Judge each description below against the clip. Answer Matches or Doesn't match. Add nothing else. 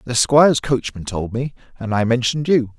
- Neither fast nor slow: Matches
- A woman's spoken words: Doesn't match